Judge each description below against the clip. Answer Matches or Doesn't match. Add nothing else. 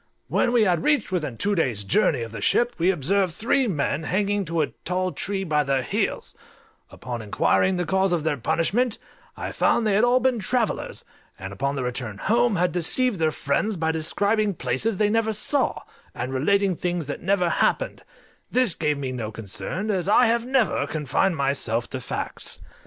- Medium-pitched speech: Matches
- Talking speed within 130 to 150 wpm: Doesn't match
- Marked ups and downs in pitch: Matches